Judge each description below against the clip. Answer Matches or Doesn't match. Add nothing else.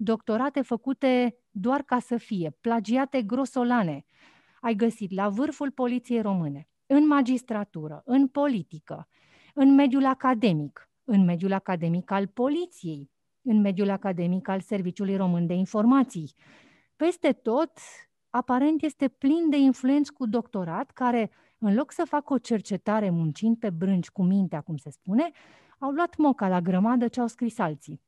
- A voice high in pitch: Matches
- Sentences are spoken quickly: Doesn't match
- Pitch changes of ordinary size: Doesn't match